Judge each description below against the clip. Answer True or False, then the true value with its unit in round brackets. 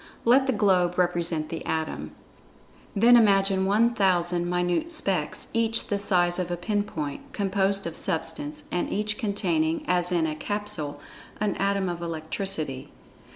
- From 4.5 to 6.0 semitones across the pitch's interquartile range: False (3.5 semitones)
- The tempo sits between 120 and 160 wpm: True (145 wpm)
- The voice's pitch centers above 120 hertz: True (185 Hz)